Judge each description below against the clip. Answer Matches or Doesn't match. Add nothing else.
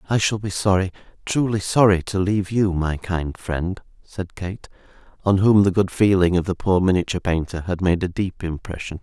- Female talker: Doesn't match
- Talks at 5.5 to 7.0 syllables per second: Doesn't match